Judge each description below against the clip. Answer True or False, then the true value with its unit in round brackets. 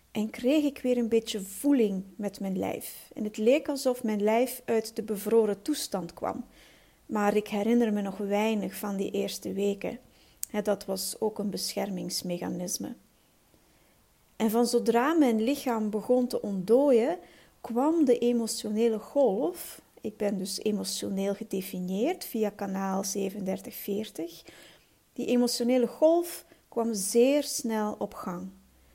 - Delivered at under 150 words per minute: True (135 wpm)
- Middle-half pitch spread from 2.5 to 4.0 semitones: True (3.2 semitones)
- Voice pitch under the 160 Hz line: False (220 Hz)